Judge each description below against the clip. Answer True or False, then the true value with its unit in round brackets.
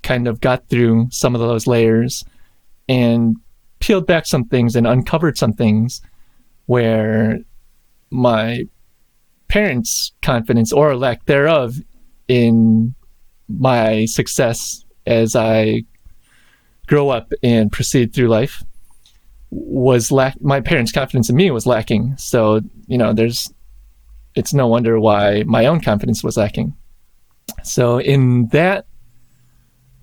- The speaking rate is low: True (120 wpm)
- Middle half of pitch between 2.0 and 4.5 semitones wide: True (2.4 semitones)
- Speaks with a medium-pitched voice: False (120 Hz)